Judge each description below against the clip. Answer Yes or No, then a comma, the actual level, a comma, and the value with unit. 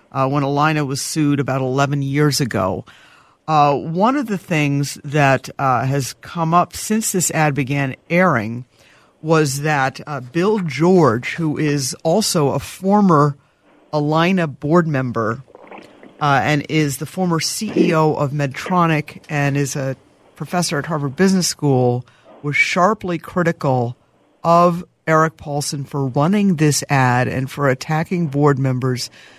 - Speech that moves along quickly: No, average, 140 wpm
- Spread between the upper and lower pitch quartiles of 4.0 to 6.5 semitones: No, average, 3.5 semitones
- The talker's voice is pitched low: No, medium, 150 Hz